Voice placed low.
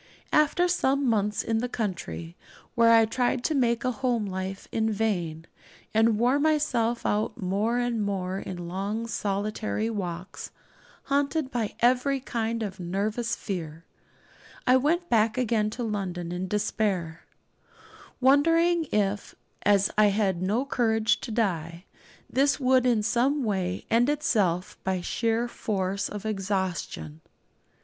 No: high, 220 Hz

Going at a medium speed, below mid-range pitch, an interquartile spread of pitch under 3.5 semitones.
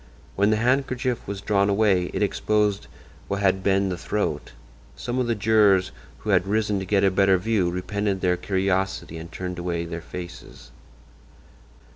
Yes: average, 165 wpm; low, 100 Hz; narrow, 2.5 semitones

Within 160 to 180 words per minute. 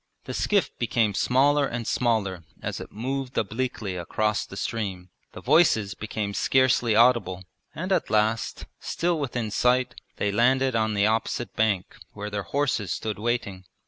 No: average, 150 wpm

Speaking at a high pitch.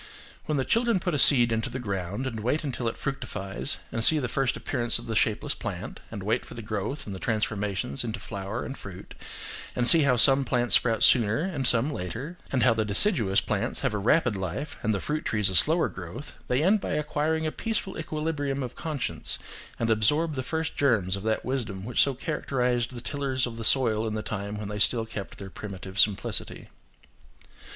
No: low, 120 Hz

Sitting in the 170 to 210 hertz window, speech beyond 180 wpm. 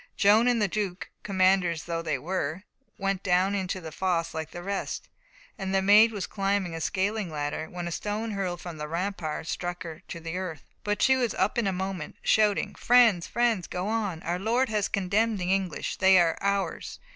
Yes: high, 190 Hz; average, 200 wpm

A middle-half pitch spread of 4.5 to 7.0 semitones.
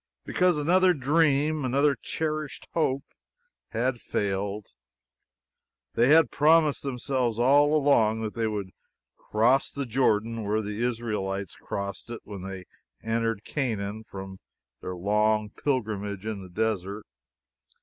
Yes: average, 5.2 semitones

